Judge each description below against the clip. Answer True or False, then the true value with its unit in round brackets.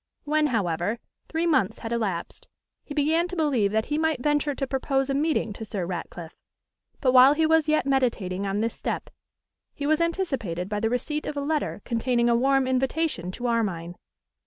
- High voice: True (260 Hz)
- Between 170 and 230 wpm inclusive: True (185 wpm)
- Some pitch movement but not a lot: False (5.9 semitones)